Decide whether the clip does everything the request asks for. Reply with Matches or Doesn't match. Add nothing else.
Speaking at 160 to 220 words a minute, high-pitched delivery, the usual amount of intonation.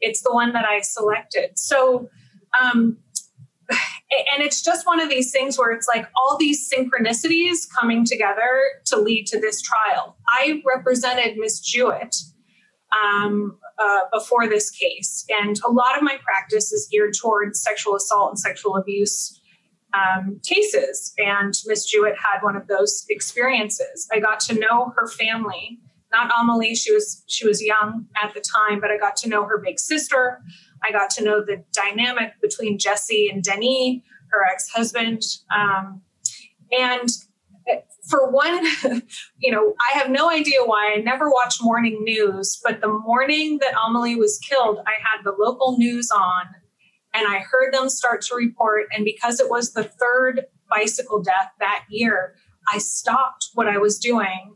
Matches